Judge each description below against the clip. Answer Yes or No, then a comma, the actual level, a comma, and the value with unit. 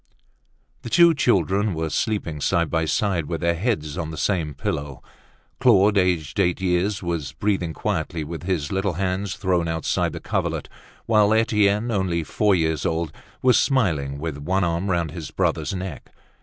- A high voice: No, very low, 90 Hz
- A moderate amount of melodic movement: Yes, average, 3.8 semitones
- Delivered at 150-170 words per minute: Yes, average, 165 wpm